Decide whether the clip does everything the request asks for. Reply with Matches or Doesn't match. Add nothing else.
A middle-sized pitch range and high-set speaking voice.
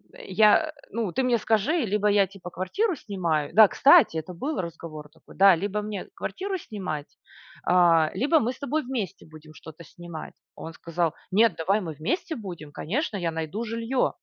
Doesn't match